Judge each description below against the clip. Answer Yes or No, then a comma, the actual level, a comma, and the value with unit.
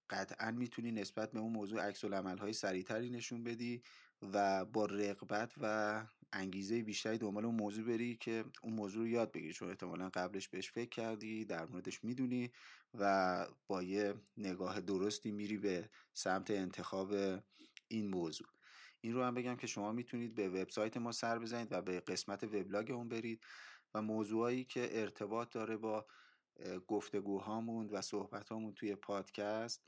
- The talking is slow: No, fast, 155 wpm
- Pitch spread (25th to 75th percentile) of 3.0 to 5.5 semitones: No, narrow, 2.6 semitones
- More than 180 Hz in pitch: No, low, 105 Hz